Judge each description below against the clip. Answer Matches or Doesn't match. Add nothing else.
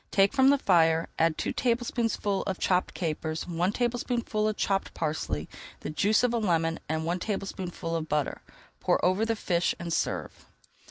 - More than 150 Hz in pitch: Matches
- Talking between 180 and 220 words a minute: Doesn't match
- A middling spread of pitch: Matches